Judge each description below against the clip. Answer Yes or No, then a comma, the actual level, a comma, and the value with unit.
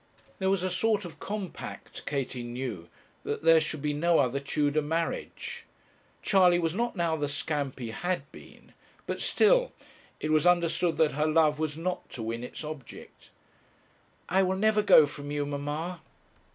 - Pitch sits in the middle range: Yes, medium, 155 Hz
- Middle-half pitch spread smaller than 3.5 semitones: No, average, 3.8 semitones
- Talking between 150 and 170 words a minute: Yes, average, 165 wpm